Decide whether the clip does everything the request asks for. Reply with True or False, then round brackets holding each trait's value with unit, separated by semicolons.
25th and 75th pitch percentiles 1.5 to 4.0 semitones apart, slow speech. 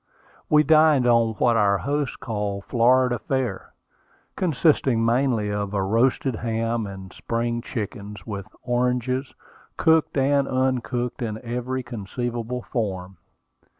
True (3.2 semitones; 115 wpm)